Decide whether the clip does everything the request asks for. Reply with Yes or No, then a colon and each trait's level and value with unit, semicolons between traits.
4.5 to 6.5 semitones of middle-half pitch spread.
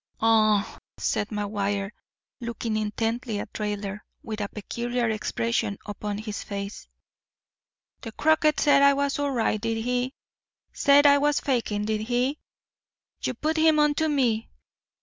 Yes: average, 4.9 semitones